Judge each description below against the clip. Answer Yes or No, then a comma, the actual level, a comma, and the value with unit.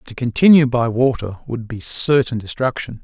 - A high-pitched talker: No, low, 120 Hz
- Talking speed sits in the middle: Yes, average, 160 wpm